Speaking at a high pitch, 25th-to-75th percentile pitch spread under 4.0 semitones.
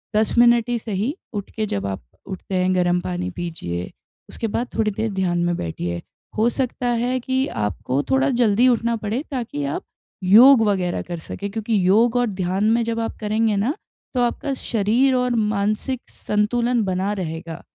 No: high, 215 Hz; average, 4.6 semitones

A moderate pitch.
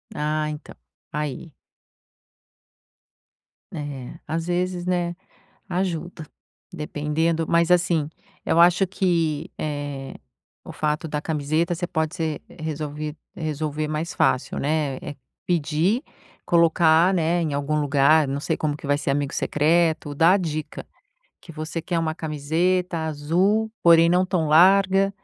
Yes: medium, 160 Hz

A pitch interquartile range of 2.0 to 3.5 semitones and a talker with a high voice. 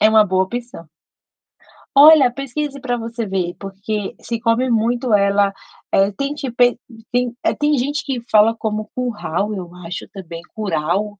No: average, 3.9 semitones; high, 220 Hz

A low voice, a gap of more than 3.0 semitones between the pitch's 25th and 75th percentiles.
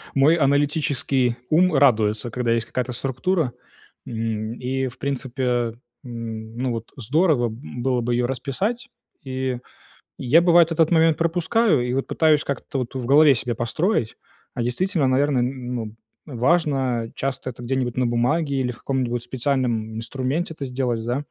Yes: low, 130 Hz; average, 3.4 semitones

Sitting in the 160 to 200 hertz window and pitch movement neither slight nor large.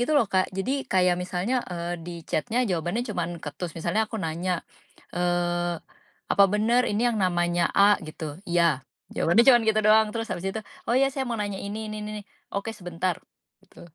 Yes: high, 190 Hz; average, 4.0 semitones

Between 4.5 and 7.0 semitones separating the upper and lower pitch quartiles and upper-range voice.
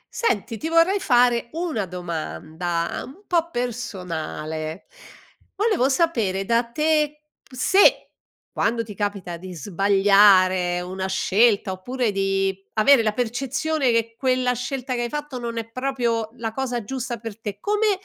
Yes: wide, 5.5 semitones; high, 230 Hz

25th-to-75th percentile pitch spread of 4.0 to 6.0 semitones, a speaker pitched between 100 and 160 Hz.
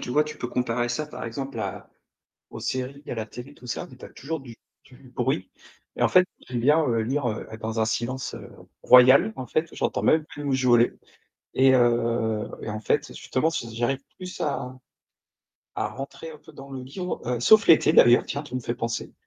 No: average, 3.2 semitones; low, 130 Hz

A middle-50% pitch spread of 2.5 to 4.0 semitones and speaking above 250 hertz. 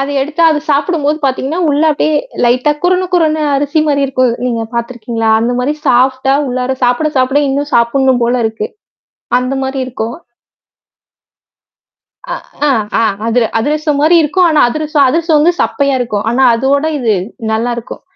Yes: average, 3.5 semitones; very high, 270 Hz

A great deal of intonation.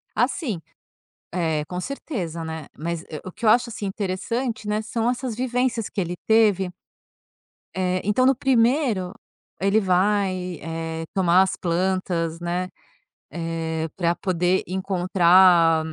No: average, 4.3 semitones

